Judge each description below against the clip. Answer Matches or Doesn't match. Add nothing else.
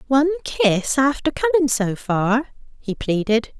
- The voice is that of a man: Doesn't match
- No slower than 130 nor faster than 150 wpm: Matches